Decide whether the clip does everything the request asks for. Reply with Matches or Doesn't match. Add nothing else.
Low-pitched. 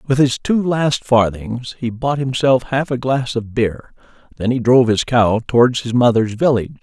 Matches